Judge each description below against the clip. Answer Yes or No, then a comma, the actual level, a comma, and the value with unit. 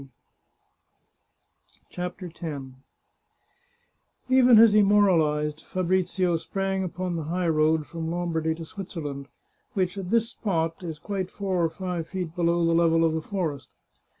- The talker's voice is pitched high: No, medium, 175 Hz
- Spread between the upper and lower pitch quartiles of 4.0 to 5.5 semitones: No, average, 2.9 semitones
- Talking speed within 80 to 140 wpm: Yes, slow, 135 wpm